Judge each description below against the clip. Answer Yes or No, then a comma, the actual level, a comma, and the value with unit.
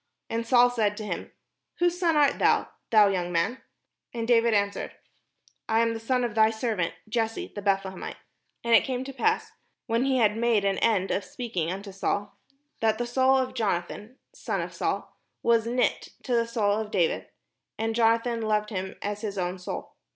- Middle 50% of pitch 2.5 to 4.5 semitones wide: Yes, average, 2.8 semitones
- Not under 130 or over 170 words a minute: No, average, 190 wpm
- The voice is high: Yes, high, 225 Hz